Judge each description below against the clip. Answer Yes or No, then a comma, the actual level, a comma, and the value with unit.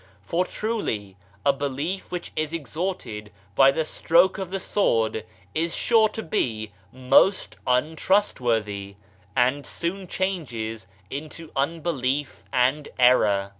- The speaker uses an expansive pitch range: Yes, wide, 6.6 semitones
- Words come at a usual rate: No, slow, 115 wpm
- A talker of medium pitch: Yes, medium, 145 Hz